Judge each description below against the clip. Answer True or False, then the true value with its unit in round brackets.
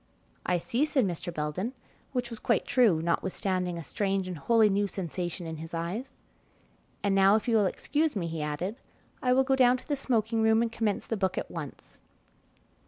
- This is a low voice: False (200 Hz)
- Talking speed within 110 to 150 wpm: False (195 wpm)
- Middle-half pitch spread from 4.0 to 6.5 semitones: True (5.1 semitones)